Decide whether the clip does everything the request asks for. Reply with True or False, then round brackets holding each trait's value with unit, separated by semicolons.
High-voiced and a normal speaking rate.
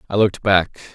False (100 Hz; 190 wpm)